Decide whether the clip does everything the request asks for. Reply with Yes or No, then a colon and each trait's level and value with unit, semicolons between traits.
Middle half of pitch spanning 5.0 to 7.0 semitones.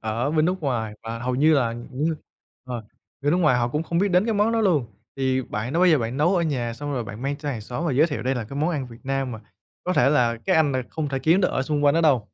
No: average, 4.5 semitones